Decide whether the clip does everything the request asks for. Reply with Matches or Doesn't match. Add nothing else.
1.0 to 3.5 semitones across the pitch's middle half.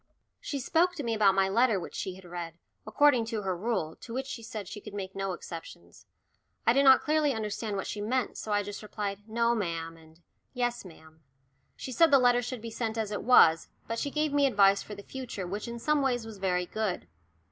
Doesn't match